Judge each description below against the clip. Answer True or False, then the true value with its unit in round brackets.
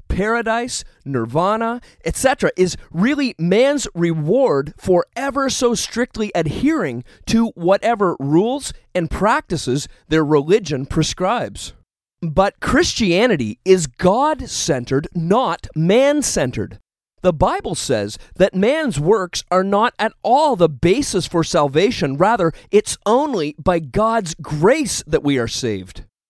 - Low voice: False (180 Hz)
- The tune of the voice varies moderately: False (6.9 semitones)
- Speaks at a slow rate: True (120 wpm)